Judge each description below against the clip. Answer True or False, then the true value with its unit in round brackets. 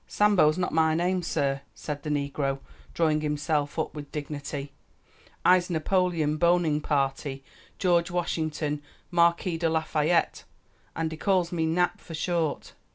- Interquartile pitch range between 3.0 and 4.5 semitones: False (2.6 semitones)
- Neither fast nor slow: False (130 wpm)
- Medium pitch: True (160 Hz)